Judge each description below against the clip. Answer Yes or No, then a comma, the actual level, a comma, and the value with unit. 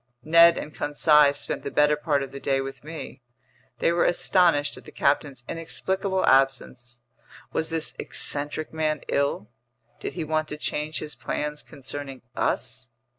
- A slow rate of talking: No, average, 155 wpm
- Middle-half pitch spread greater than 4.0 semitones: No, narrow, 2.5 semitones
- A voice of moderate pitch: Yes, medium, 150 Hz